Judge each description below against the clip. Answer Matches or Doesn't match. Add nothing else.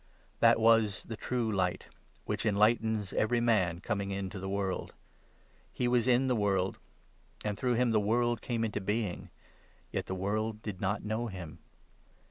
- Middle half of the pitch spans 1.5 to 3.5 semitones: Matches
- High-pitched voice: Doesn't match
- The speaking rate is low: Doesn't match